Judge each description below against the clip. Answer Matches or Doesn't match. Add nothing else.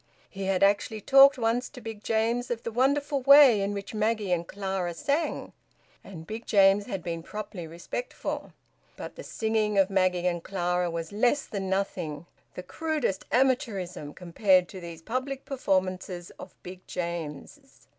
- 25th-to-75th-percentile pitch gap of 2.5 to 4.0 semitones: Doesn't match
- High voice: Matches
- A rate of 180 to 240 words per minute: Doesn't match